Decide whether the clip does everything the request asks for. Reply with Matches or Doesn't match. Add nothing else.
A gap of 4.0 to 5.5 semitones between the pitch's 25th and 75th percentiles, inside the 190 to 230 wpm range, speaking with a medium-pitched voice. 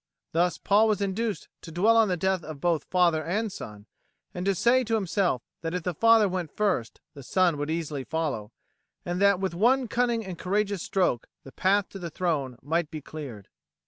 Matches